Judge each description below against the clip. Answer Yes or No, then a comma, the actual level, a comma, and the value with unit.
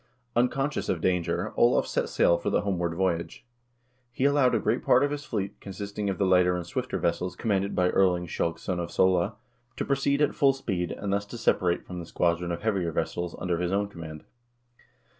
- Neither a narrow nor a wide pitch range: Yes, average, 3.8 semitones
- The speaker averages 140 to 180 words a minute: No, fast, 205 wpm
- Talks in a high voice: No, very low, 95 Hz